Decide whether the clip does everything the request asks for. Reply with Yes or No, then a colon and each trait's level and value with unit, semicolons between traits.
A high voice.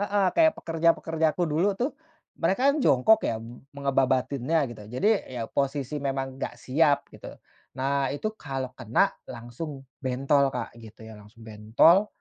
No: medium, 140 Hz